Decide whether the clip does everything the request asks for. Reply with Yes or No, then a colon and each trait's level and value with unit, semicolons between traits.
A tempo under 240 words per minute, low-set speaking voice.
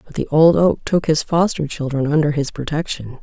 No: fast, 205 wpm; medium, 150 Hz